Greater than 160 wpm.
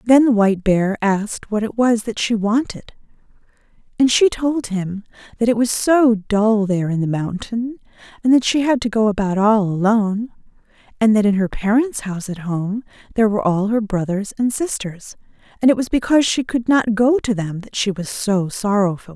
Yes: average, 195 wpm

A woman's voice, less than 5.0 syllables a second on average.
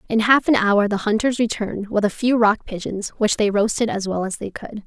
No: female; 5.5 syllables/s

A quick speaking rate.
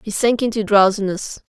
No: average, 160 wpm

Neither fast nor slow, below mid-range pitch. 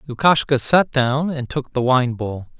Yes: average, 185 wpm; low, 130 Hz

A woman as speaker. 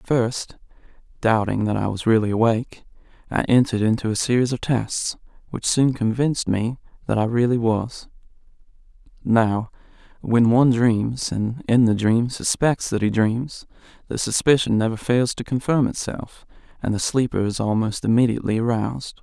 No: male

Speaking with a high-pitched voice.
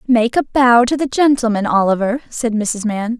Yes: high, 235 Hz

